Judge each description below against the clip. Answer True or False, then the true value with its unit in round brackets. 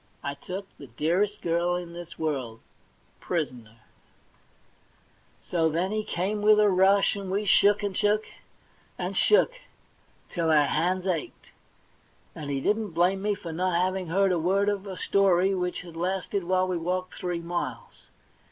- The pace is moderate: True (165 wpm)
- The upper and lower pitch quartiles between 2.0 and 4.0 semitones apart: True (2.8 semitones)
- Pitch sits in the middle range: True (180 Hz)